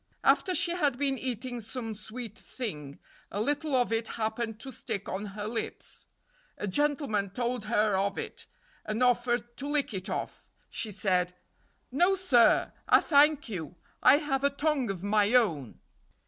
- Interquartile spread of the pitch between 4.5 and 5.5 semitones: Yes, average, 4.8 semitones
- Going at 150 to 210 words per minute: Yes, average, 160 wpm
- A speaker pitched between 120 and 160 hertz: No, high, 235 Hz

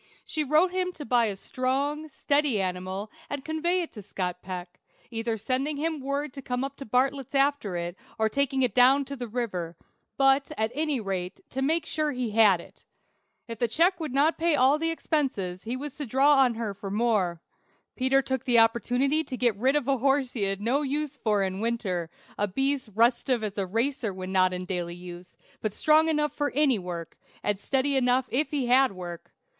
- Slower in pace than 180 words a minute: No, average, 200 wpm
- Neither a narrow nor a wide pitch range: No, wide, 5.7 semitones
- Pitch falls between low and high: No, very high, 250 Hz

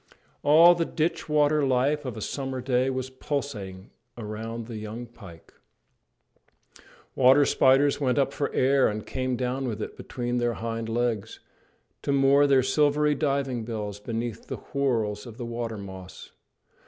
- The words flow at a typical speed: Yes, average, 155 wpm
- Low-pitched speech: Yes, low, 125 Hz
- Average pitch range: Yes, average, 3.7 semitones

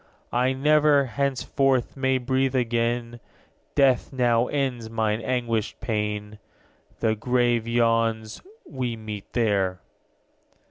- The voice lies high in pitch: No, low, 120 Hz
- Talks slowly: Yes, slow, 100 wpm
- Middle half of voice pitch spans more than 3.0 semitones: No, average, 2.7 semitones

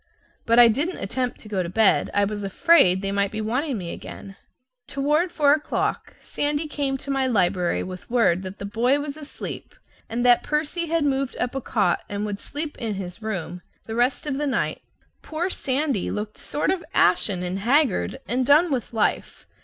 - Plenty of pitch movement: Yes, wide, 6.3 semitones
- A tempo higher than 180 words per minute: Yes, average, 195 wpm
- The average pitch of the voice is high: Yes, high, 245 Hz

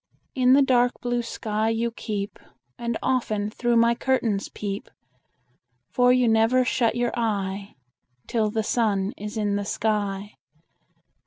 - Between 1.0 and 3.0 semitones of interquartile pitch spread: Yes, average, 2.7 semitones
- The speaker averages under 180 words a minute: Yes, average, 140 wpm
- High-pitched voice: Yes, high, 225 Hz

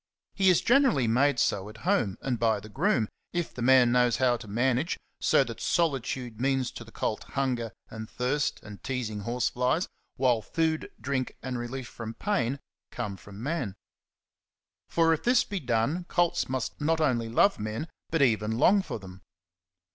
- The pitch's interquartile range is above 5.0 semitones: Yes, wide, 5.4 semitones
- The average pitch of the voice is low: Yes, low, 125 Hz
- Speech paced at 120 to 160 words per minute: No, average, 170 wpm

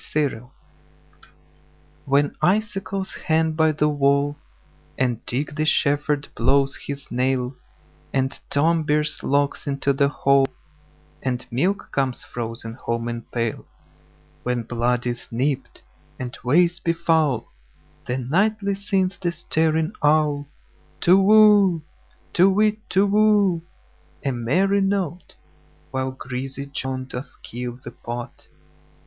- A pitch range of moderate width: Yes, average, 5.0 semitones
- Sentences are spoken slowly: Yes, slow, 105 wpm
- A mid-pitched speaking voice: Yes, medium, 145 Hz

